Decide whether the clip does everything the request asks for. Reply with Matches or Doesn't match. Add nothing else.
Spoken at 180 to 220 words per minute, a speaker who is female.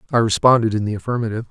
Doesn't match